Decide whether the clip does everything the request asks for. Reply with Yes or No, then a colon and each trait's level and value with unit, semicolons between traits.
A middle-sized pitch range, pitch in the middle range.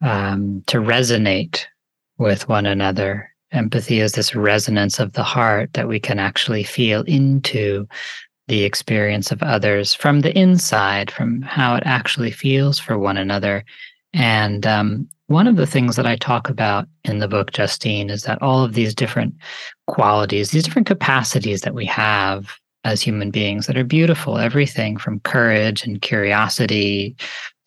No: average, 4.3 semitones; low, 110 Hz